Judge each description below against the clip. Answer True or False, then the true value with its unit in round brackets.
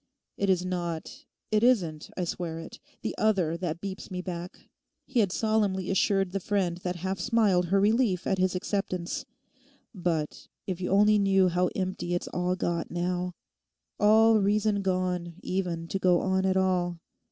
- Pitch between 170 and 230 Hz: True (185 Hz)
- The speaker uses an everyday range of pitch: False (2.2 semitones)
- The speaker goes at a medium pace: True (155 wpm)